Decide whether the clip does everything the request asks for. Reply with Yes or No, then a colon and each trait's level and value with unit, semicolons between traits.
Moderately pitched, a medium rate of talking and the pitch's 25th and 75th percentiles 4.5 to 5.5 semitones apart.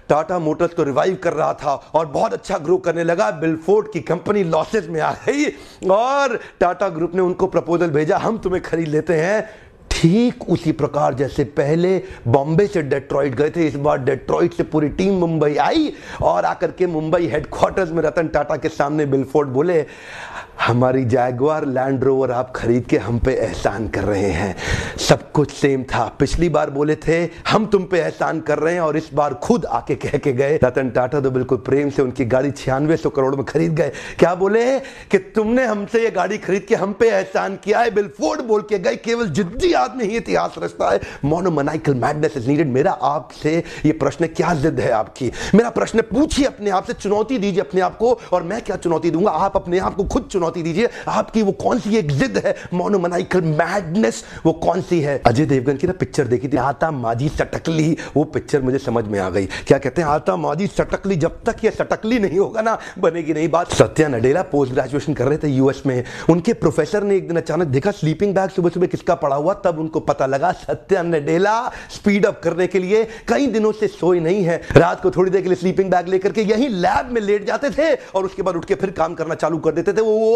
Yes: medium, 170 Hz; average, 150 wpm; average, 5.2 semitones